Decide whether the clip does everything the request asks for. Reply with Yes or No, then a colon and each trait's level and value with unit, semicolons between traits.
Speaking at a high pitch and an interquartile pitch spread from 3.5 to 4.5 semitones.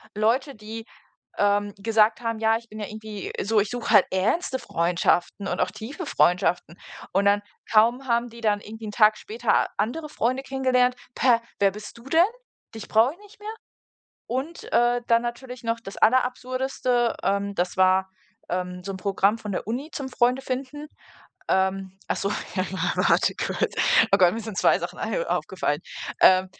Yes: high, 225 Hz; average, 3.9 semitones